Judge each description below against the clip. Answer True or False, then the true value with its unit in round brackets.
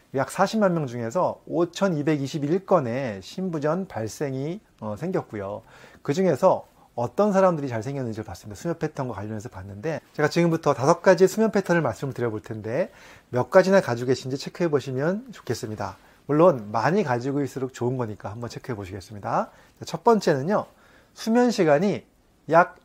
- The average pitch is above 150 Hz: False (140 Hz)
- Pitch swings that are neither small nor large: False (7.3 semitones)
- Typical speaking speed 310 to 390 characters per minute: True (345 characters per minute)